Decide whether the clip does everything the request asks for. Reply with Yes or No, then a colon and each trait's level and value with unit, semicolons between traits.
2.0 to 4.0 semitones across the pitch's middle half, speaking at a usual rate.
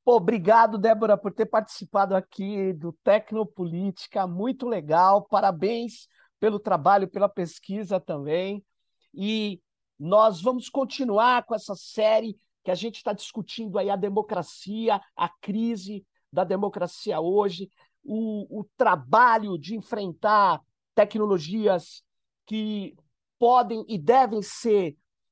No: narrow, 2.4 semitones; slow, 110 wpm